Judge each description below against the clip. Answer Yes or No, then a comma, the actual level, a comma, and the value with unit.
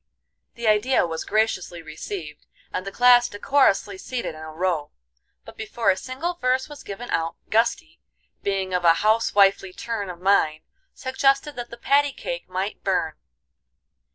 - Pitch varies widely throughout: Yes, wide, 5.7 semitones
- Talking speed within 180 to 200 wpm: No, average, 155 wpm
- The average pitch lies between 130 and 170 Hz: No, high, 205 Hz